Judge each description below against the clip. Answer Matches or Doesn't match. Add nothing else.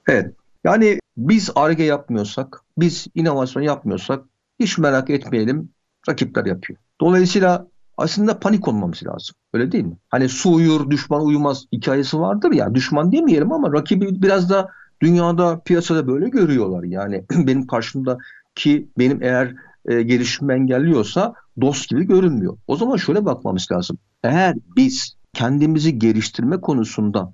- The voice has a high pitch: Doesn't match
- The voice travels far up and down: Matches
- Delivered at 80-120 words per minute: Doesn't match